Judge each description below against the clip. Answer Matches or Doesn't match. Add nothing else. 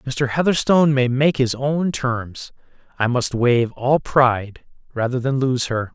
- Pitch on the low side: Matches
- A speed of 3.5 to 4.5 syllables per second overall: Matches